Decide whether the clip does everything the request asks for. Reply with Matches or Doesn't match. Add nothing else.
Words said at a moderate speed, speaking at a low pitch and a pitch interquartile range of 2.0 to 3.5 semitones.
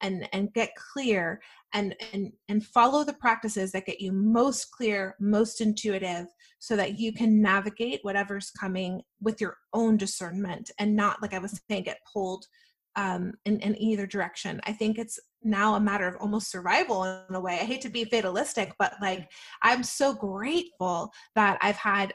Doesn't match